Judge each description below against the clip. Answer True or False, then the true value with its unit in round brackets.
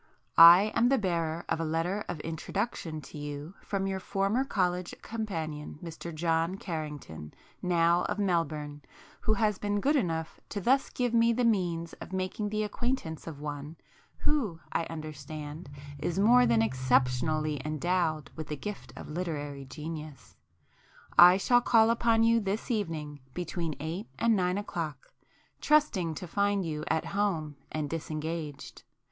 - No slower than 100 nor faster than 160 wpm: True (150 wpm)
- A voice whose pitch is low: False (170 Hz)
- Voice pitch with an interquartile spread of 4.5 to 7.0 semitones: True (4.9 semitones)